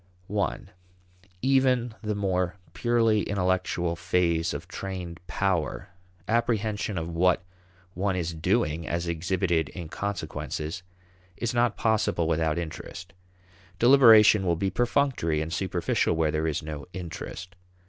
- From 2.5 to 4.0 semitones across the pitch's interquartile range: No, average, 4.4 semitones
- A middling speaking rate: No, slow, 120 wpm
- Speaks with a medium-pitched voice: No, very low, 90 Hz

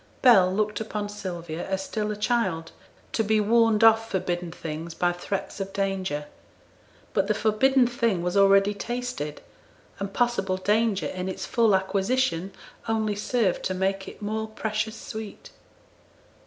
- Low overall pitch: No, high, 205 Hz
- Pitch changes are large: No, average, 2.8 semitones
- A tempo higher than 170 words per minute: No, average, 145 wpm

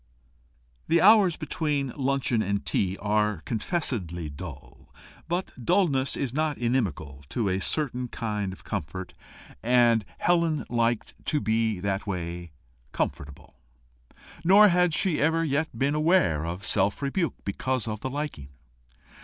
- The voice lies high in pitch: No, low, 120 Hz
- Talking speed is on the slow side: Yes, slow, 130 wpm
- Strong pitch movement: Yes, wide, 7.9 semitones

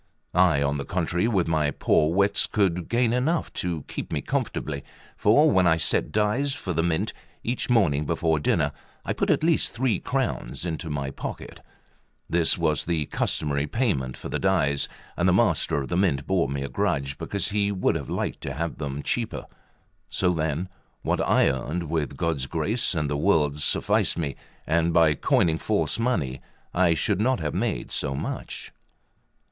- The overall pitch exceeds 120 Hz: No, very low, 85 Hz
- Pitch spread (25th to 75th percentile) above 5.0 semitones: Yes, wide, 5.5 semitones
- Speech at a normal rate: Yes, average, 180 wpm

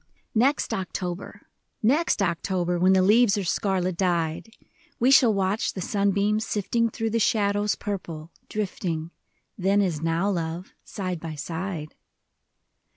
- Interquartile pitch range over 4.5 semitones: No, average, 3.2 semitones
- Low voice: No, high, 190 Hz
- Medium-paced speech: No, slow, 130 wpm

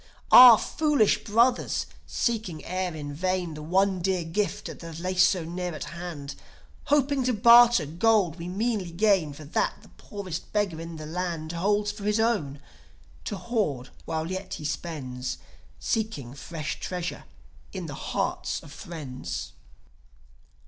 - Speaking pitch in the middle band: Yes, medium, 180 Hz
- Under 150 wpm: Yes, average, 140 wpm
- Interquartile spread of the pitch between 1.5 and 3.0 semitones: No, average, 4.8 semitones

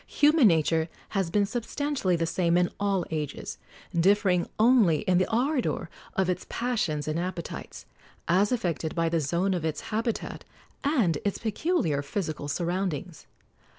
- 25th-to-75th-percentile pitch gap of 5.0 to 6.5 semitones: No, average, 4.6 semitones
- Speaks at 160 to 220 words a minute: No, average, 145 wpm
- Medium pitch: Yes, medium, 180 Hz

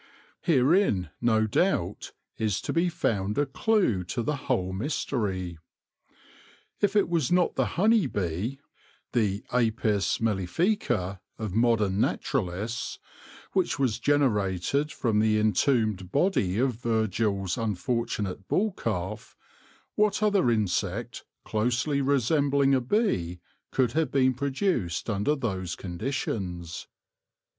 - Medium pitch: No, low, 115 Hz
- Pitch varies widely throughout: Yes, wide, 6.2 semitones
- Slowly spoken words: Yes, slow, 115 wpm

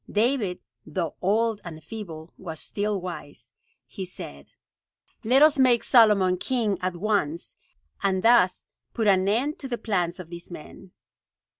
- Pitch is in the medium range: No, high, 195 Hz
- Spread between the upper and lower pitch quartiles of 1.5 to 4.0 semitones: No, average, 4.5 semitones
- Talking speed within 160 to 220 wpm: No, average, 145 wpm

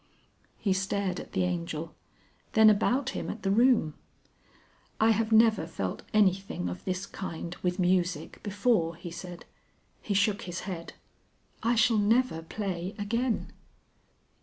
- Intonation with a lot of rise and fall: No, average, 3.9 semitones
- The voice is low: No, high, 195 Hz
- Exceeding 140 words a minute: No, slow, 135 wpm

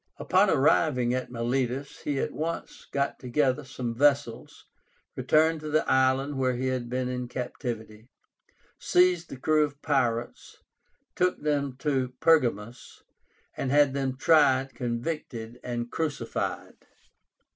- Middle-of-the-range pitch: No, low, 130 Hz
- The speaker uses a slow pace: Yes, slow, 125 wpm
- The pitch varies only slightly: No, average, 3.0 semitones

